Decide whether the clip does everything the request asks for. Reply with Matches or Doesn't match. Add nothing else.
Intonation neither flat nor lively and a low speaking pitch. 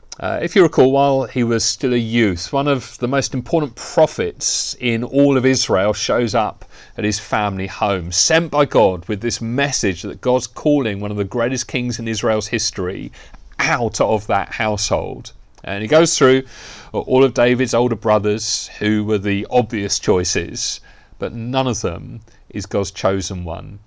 Matches